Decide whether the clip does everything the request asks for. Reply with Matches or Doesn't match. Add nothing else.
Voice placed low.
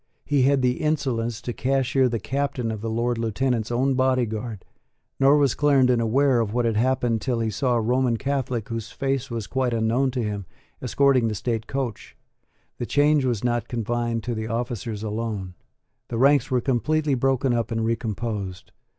Matches